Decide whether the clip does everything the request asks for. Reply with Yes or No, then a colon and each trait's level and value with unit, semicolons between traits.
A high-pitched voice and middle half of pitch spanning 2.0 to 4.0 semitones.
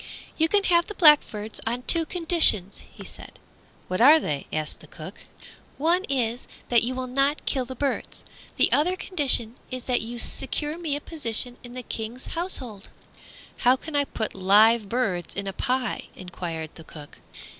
No: very high, 250 Hz; wide, 5.6 semitones